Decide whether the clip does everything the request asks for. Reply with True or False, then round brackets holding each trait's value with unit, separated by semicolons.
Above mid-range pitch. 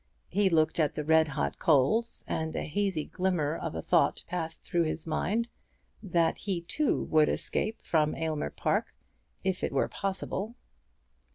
False (165 Hz)